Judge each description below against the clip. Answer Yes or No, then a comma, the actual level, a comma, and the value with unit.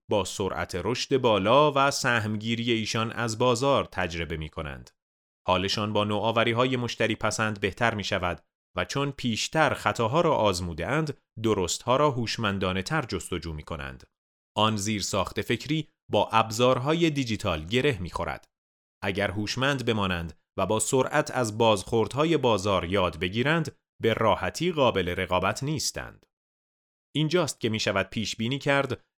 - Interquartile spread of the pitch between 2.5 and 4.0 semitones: No, average, 4.9 semitones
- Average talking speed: Yes, average, 140 wpm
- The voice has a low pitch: Yes, low, 110 Hz